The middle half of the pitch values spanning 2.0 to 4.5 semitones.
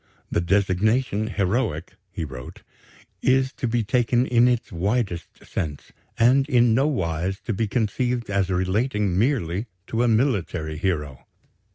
No: average, 5.3 semitones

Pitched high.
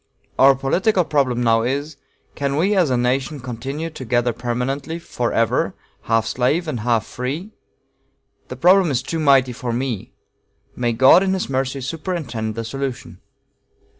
No: low, 130 Hz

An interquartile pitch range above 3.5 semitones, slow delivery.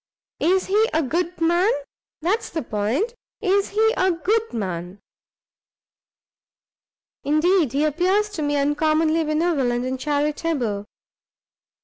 Yes: average, 5.0 semitones; slow, 110 wpm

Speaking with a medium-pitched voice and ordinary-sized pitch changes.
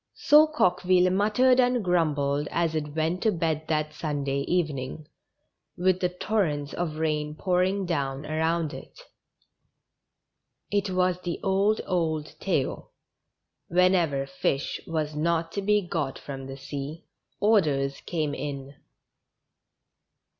Yes: medium, 165 Hz; average, 3.7 semitones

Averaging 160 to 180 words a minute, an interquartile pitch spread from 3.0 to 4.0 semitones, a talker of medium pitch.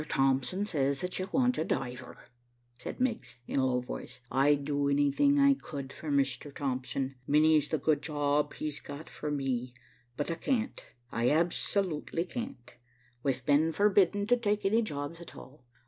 No: average, 165 wpm; wide, 5.5 semitones; medium, 150 Hz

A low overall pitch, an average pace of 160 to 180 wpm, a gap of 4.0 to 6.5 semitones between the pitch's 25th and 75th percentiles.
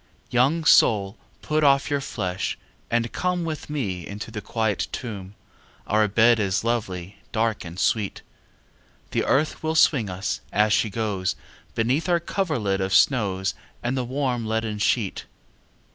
No: low, 110 Hz; average, 150 wpm; average, 5.3 semitones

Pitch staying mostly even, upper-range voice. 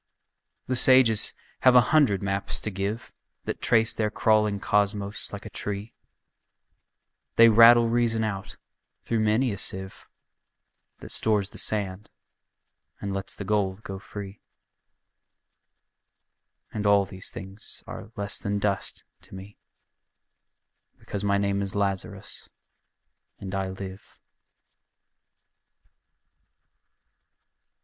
No: narrow, 2.0 semitones; low, 100 Hz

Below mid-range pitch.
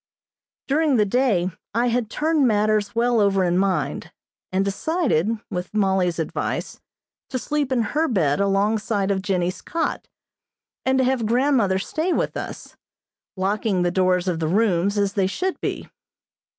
No: high, 205 Hz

